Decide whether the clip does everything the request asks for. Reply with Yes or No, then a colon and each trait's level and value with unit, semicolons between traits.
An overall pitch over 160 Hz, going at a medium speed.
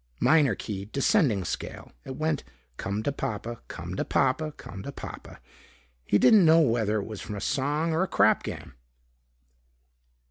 No: low, 130 Hz; average, 165 wpm